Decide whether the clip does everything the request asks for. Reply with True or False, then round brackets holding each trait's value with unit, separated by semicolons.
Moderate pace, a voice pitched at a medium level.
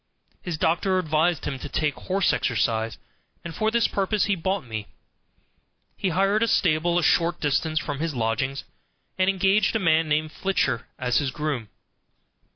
True (160 wpm; 160 Hz)